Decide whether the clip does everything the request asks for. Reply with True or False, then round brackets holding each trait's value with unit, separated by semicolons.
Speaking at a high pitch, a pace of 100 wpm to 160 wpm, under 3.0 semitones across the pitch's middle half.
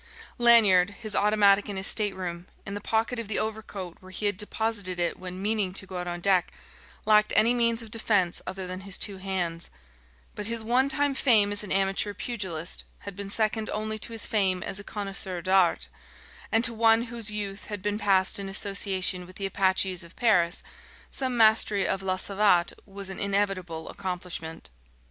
False (200 Hz; 185 wpm; 2.6 semitones)